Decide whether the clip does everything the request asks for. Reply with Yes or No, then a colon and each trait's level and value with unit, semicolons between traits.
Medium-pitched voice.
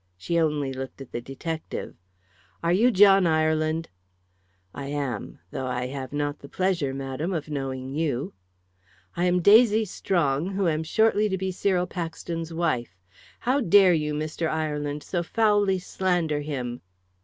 Yes: medium, 160 Hz